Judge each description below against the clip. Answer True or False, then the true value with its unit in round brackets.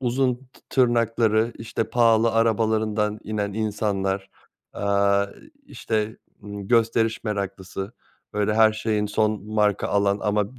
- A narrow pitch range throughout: True (1.9 semitones)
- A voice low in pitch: True (110 Hz)